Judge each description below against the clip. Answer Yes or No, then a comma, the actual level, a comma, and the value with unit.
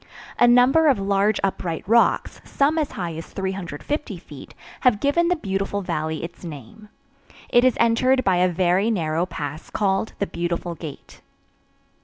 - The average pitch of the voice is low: No, high, 195 Hz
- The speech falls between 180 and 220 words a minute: No, average, 155 wpm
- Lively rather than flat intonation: Yes, wide, 5.9 semitones